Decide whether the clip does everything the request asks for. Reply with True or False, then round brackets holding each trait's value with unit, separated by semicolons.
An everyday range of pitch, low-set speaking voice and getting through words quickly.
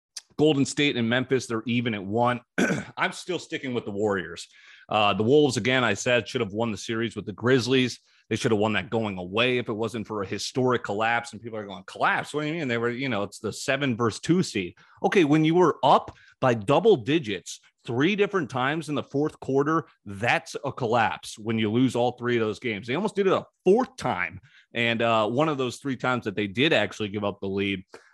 True (3.8 semitones; 120 Hz; 230 wpm)